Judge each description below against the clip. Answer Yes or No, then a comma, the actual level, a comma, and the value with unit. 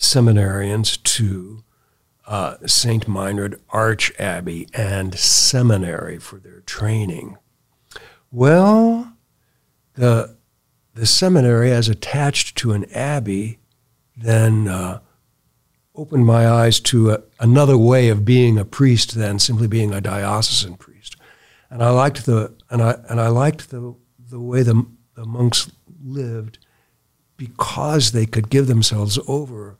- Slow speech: Yes, slow, 125 wpm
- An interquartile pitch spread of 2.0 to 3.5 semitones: Yes, average, 2.9 semitones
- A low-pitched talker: Yes, low, 115 Hz